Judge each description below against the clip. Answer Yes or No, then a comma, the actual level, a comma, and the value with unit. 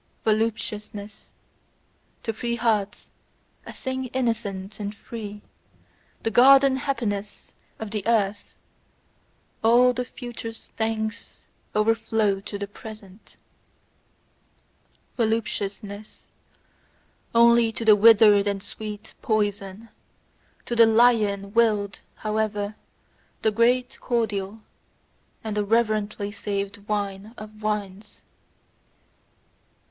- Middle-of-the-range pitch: No, high, 215 Hz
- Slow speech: Yes, slow, 90 wpm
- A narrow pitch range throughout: Yes, narrow, 2.1 semitones